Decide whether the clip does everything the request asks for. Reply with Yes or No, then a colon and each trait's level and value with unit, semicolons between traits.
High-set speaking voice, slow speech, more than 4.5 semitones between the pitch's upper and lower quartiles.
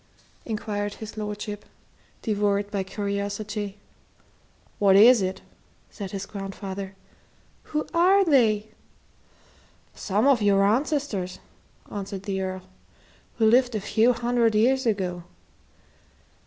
No: high, 210 Hz; slow, 105 wpm; narrow, 2.6 semitones